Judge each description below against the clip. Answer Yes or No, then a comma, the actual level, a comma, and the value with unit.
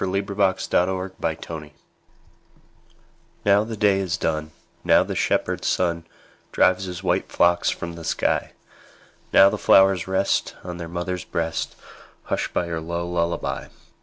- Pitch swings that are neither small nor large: No, narrow, 2.3 semitones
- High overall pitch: No, very low, 90 Hz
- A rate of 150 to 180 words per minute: No, average, 140 wpm